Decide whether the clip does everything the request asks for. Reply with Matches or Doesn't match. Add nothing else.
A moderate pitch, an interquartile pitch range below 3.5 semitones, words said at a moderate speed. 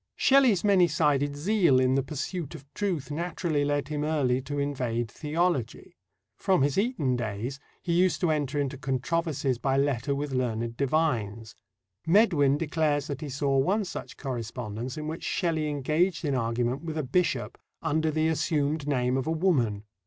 Doesn't match